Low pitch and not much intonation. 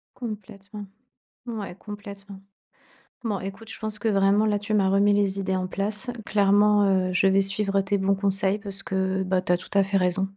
No: high, 200 Hz; narrow, 1.3 semitones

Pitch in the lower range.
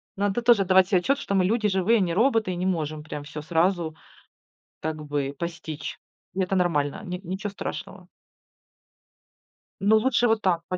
No: medium, 185 Hz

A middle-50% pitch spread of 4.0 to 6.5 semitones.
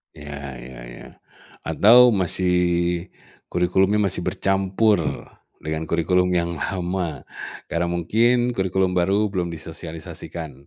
No: average, 2.7 semitones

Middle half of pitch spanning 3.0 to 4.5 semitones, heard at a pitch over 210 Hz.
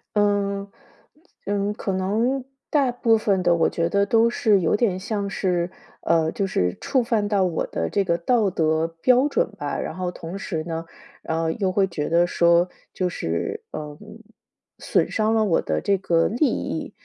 No: average, 3.8 semitones; high, 190 Hz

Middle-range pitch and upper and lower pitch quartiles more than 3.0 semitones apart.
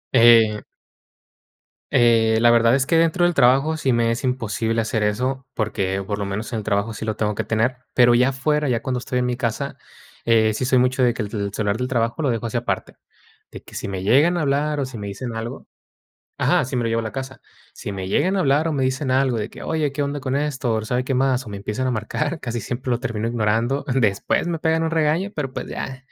No: low, 125 Hz; average, 3.4 semitones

